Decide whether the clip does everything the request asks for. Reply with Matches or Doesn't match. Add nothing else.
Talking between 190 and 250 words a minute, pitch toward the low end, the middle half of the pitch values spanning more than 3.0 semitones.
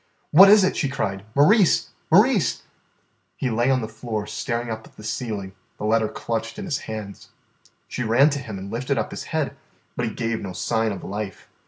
Matches